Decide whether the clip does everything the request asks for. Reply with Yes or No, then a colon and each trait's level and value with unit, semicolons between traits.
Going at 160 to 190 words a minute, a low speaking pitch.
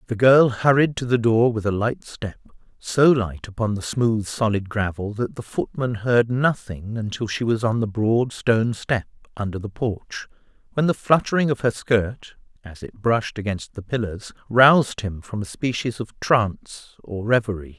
Yes: average, 180 wpm; low, 115 Hz